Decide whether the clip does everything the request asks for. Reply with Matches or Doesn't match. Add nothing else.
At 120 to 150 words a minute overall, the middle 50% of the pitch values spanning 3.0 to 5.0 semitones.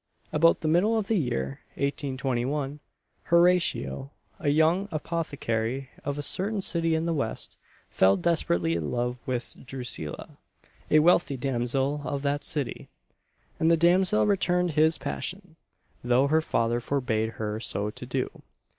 Doesn't match